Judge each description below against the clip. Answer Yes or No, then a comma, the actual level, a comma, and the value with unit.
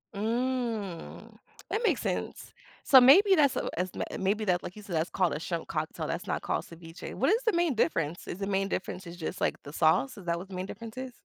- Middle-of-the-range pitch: No, high, 195 Hz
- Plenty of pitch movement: Yes, wide, 6.7 semitones